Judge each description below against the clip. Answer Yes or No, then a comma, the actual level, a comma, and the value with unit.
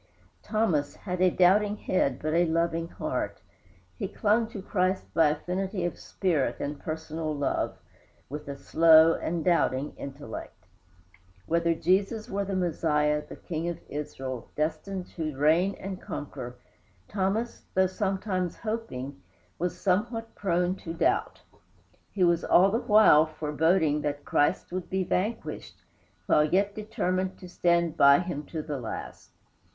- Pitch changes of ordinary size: Yes, average, 4.0 semitones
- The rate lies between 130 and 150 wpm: Yes, average, 140 wpm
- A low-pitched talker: No, medium, 170 Hz